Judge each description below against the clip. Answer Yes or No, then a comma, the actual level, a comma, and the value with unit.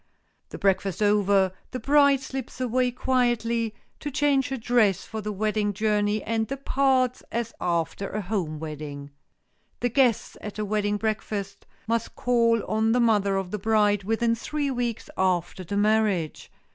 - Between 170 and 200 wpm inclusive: No, average, 155 wpm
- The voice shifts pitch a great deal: No, average, 3.4 semitones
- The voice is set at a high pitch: Yes, high, 220 Hz